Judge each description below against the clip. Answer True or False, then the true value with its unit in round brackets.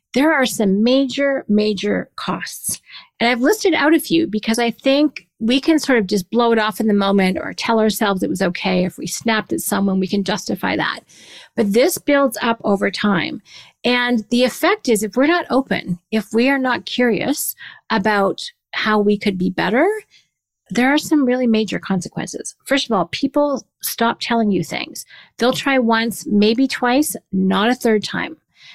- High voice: True (230 Hz)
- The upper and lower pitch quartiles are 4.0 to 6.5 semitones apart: True (4.4 semitones)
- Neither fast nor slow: True (185 wpm)